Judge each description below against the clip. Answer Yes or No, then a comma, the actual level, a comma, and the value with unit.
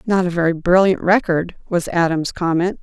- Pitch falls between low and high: Yes, medium, 175 Hz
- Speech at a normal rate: Yes, average, 170 wpm